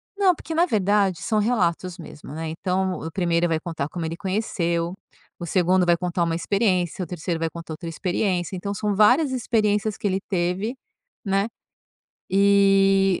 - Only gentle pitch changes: No, average, 3.1 semitones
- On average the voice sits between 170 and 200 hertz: Yes, medium, 185 Hz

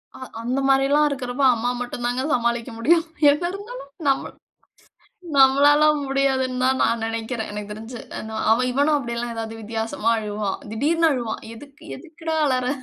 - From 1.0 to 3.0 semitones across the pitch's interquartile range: No, average, 3.8 semitones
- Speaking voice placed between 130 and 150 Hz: No, very high, 255 Hz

